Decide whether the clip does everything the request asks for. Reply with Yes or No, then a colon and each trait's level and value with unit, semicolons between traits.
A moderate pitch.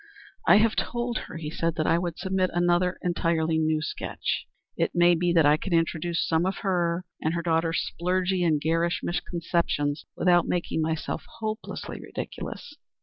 Yes: medium, 170 Hz